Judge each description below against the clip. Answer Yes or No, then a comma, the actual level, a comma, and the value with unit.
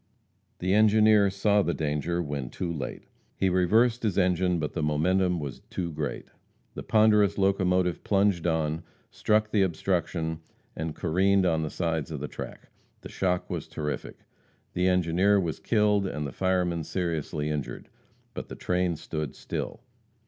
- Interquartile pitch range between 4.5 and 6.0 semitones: No, average, 3.5 semitones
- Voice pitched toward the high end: No, very low, 90 Hz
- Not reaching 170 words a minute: Yes, average, 155 wpm